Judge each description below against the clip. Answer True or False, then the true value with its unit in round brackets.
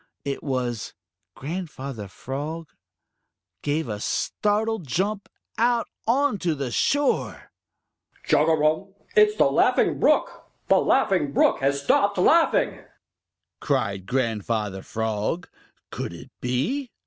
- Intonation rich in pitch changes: True (8.6 semitones)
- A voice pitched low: False (150 Hz)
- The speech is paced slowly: True (110 wpm)